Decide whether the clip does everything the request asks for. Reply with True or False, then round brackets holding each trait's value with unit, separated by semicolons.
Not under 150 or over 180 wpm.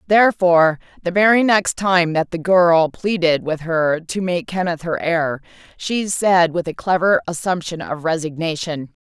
True (160 wpm)